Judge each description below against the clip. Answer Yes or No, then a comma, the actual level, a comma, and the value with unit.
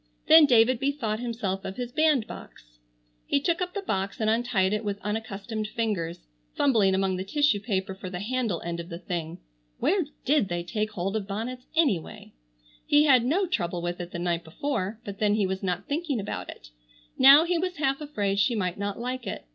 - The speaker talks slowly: No, average, 200 wpm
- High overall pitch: Yes, high, 215 Hz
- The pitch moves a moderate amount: No, wide, 5.9 semitones